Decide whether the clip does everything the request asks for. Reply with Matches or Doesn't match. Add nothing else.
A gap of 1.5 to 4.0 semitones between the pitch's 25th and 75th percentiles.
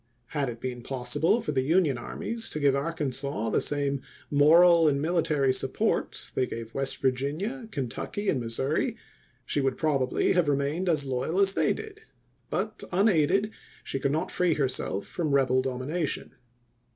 Doesn't match